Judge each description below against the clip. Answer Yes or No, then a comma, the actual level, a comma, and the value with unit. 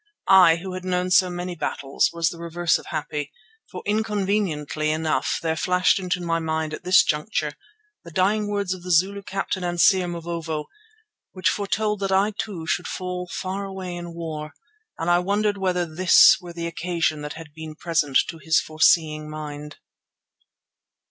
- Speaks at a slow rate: No, average, 170 wpm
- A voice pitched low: No, medium, 175 Hz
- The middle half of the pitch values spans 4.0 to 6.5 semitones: No, average, 2.8 semitones